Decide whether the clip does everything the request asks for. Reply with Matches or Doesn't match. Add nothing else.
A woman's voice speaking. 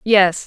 Matches